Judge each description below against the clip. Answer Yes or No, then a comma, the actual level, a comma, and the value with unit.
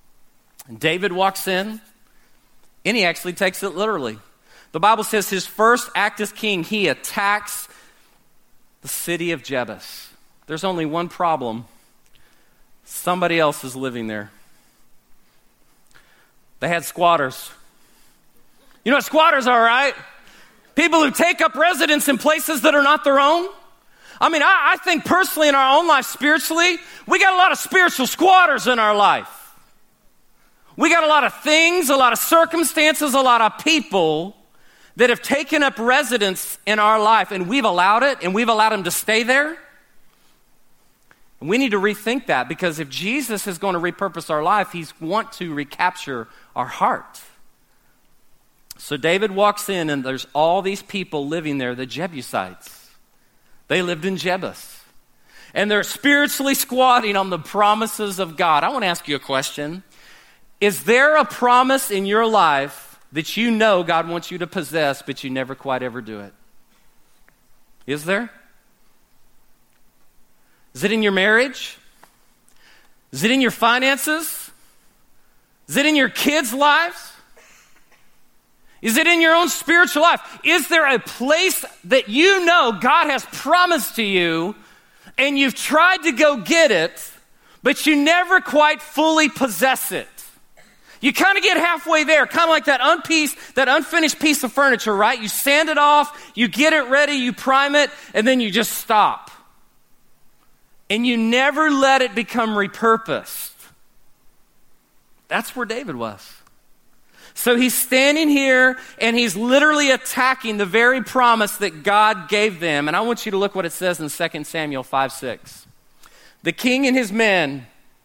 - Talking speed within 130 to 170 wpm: Yes, average, 160 wpm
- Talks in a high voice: Yes, high, 230 Hz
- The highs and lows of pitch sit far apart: Yes, wide, 8.3 semitones